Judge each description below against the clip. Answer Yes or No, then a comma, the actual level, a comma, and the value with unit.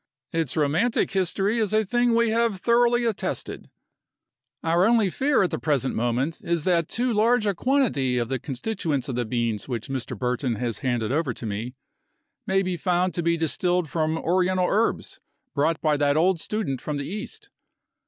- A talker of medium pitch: Yes, medium, 170 Hz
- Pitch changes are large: Yes, wide, 7.8 semitones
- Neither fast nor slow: Yes, average, 180 wpm